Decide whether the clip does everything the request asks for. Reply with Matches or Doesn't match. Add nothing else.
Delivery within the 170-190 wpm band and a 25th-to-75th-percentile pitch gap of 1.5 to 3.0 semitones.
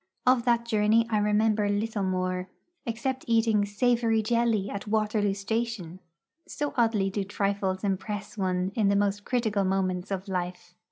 Doesn't match